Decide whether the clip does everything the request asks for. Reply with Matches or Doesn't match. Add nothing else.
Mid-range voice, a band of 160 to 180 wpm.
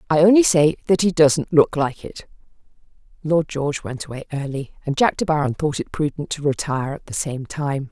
Doesn't match